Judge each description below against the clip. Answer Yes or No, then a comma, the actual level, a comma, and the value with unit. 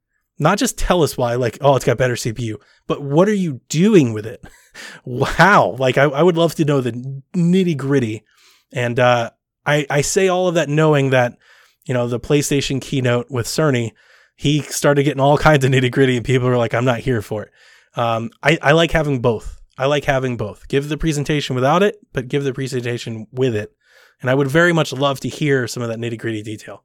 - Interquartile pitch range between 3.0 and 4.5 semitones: Yes, average, 3.5 semitones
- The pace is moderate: No, fast, 220 wpm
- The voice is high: No, low, 135 Hz